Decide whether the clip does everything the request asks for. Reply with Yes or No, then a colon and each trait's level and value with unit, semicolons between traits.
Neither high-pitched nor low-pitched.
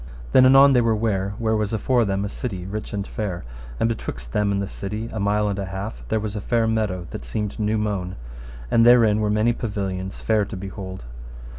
No: low, 105 Hz